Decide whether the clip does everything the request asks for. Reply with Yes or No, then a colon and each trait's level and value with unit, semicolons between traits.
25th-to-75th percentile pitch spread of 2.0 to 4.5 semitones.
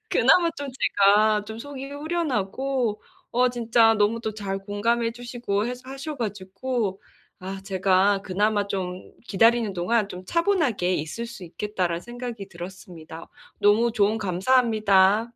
Yes: average, 3.8 semitones